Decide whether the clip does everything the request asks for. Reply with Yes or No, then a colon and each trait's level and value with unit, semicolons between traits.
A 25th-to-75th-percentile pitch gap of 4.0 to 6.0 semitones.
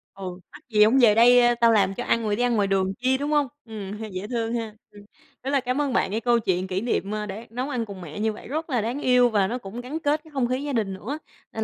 No: average, 3.6 semitones